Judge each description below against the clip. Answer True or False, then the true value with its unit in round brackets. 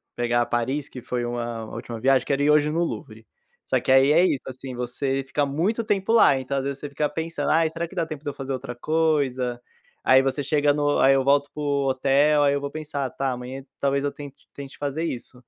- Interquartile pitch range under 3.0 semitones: True (2.4 semitones)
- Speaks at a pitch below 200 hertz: True (140 Hz)